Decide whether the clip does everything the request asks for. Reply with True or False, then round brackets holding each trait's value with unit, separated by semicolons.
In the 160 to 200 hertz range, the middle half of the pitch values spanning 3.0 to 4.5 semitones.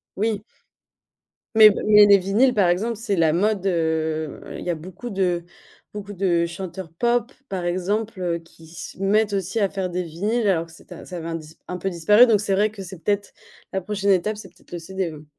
True (190 Hz; 3.4 semitones)